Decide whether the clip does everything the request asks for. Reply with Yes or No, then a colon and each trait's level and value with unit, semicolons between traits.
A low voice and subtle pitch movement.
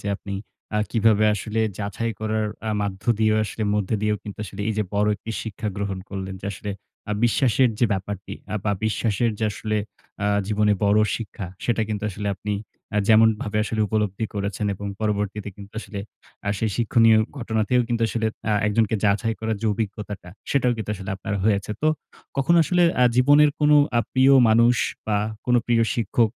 Yes: low, 110 Hz; narrow, 2.0 semitones